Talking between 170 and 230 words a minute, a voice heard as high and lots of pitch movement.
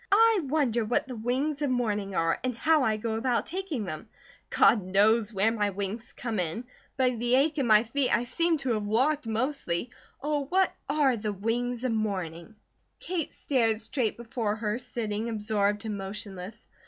No: average, 180 wpm; high, 230 Hz; average, 4.0 semitones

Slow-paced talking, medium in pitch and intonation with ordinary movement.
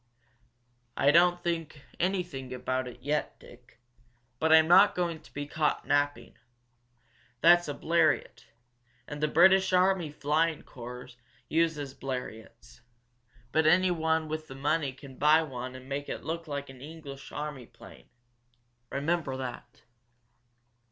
Yes: slow, 130 wpm; medium, 150 Hz; average, 3.5 semitones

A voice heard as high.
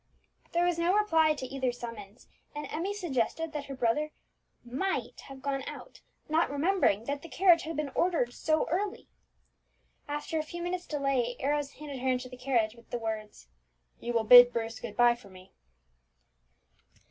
Yes: very high, 275 Hz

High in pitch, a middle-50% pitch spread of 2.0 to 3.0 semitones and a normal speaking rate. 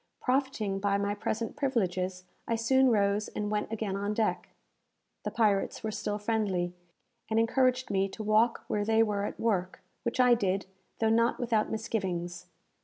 Yes: high, 215 Hz; narrow, 2.6 semitones; average, 165 wpm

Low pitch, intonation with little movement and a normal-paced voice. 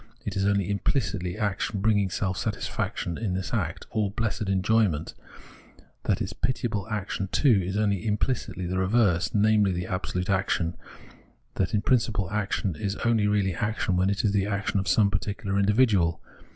Yes: low, 100 Hz; narrow, 2.3 semitones; average, 160 wpm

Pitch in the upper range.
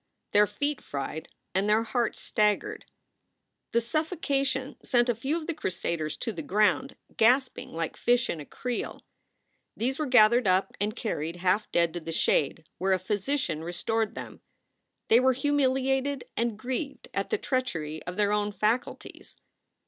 Yes: high, 225 Hz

